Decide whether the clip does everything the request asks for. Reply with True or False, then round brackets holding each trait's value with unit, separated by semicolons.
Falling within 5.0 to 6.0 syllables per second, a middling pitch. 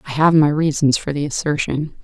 True (5.3 syllables/s; 145 Hz)